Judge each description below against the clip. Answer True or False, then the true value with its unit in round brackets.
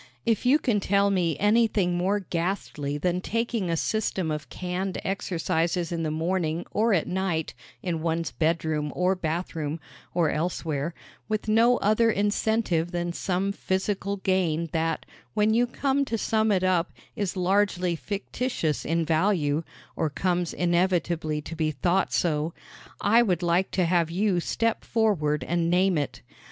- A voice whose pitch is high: False (180 Hz)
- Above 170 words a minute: False (150 wpm)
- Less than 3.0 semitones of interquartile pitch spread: False (3.6 semitones)